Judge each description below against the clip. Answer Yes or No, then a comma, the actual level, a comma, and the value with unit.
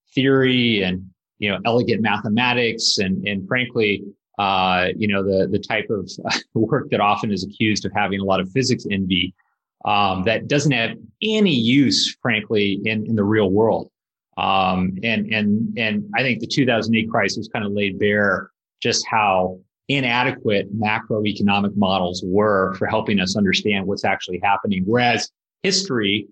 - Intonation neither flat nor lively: Yes, average, 3.5 semitones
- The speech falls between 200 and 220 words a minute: No, average, 155 wpm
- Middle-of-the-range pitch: No, low, 105 Hz